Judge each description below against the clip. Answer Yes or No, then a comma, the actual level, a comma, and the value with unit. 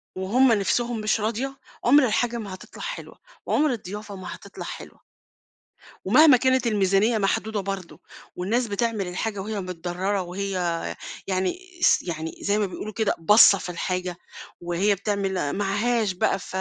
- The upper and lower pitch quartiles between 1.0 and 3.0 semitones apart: No, average, 3.5 semitones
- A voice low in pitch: No, high, 205 Hz